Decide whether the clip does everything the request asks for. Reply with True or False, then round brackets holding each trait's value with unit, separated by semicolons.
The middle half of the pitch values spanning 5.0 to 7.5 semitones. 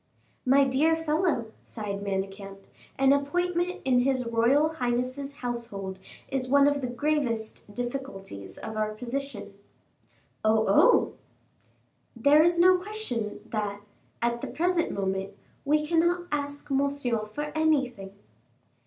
True (5.6 semitones)